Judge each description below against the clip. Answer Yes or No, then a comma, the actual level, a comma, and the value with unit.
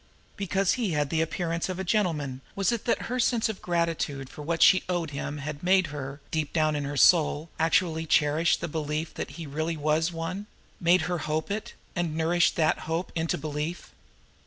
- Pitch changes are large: No, average, 2.9 semitones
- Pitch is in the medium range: Yes, medium, 165 Hz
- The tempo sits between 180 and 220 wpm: Yes, average, 195 wpm